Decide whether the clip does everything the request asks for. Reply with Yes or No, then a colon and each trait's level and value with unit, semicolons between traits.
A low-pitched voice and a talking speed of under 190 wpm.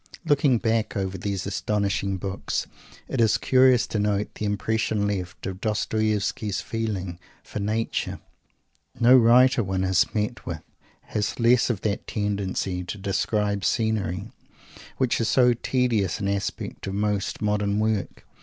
Yes: low, 105 Hz; average, 140 wpm